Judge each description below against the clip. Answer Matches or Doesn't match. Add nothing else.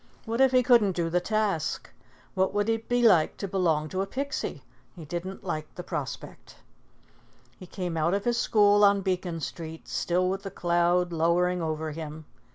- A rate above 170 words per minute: Matches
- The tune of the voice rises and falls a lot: Doesn't match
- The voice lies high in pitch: Doesn't match